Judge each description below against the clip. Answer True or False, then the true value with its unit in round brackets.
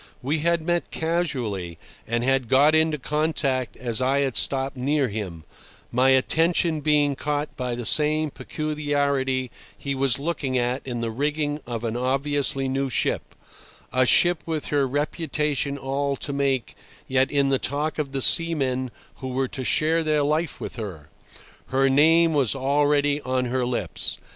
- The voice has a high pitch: False (140 Hz)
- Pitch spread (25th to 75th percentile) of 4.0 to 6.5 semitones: False (2.7 semitones)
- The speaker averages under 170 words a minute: True (160 wpm)